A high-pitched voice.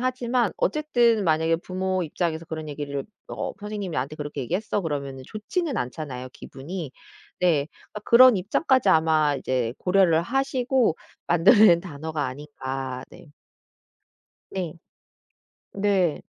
No: medium, 170 Hz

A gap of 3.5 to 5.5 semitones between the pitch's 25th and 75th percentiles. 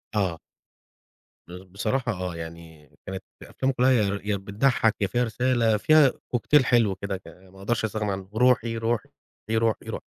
Yes: average, 4.1 semitones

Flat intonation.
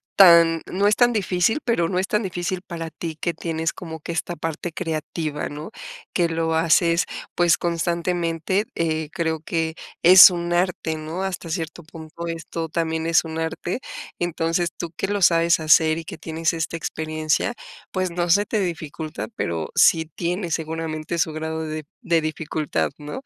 Yes: narrow, 1.6 semitones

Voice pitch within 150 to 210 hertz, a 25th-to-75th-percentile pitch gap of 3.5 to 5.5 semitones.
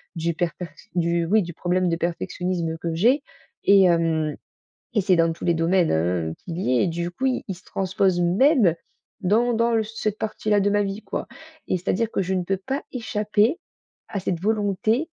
Yes: medium, 185 Hz; average, 3.9 semitones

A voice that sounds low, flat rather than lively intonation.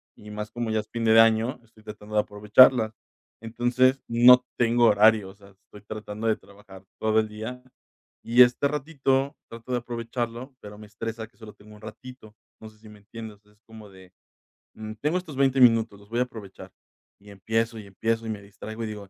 Yes: low, 110 Hz; narrow, 2.2 semitones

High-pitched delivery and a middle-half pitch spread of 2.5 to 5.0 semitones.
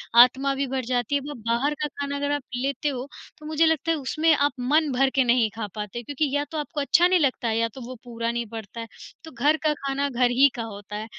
Yes: very high, 270 Hz; average, 3.5 semitones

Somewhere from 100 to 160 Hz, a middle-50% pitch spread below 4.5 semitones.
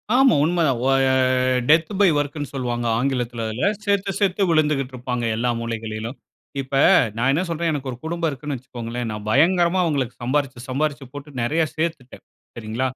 No: low, 135 Hz; average, 4.8 semitones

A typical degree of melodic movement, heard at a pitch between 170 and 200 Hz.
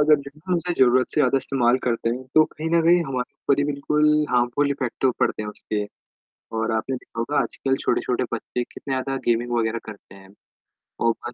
No: average, 3.6 semitones; low, 130 Hz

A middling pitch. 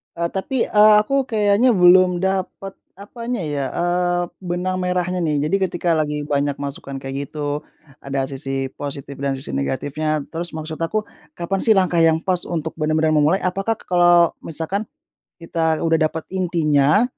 Yes: medium, 165 Hz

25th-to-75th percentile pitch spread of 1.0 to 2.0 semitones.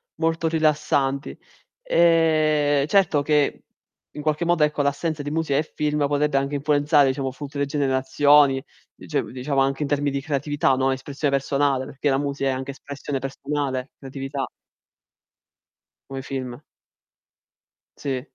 Yes: narrow, 1.7 semitones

